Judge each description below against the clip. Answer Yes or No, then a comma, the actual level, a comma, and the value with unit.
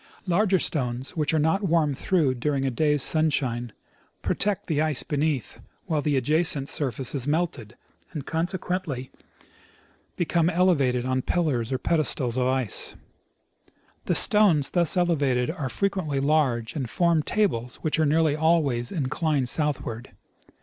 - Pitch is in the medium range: Yes, medium, 150 Hz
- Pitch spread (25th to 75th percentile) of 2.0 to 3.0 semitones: No, average, 4.4 semitones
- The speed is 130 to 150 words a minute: Yes, slow, 135 wpm